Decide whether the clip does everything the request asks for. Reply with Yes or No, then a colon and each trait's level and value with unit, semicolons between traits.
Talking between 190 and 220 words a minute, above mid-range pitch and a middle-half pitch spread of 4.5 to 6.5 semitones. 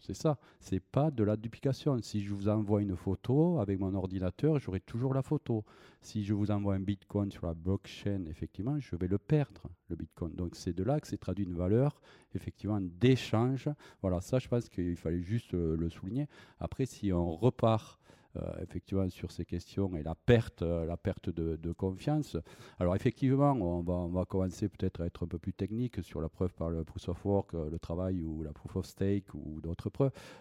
No: average, 210 wpm; very low, 95 Hz; average, 4.8 semitones